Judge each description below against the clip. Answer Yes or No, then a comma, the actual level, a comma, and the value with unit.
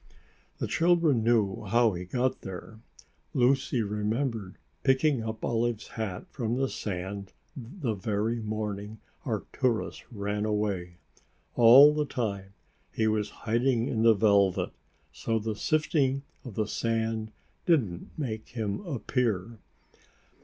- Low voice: Yes, low, 110 Hz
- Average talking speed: No, slow, 120 wpm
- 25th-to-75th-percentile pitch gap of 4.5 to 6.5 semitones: No, average, 3.2 semitones